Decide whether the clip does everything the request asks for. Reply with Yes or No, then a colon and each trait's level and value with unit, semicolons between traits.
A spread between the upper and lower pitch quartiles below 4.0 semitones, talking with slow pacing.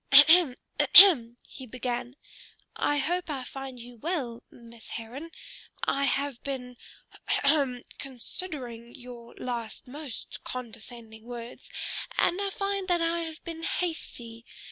No: average, 5.1 semitones; slow, 125 wpm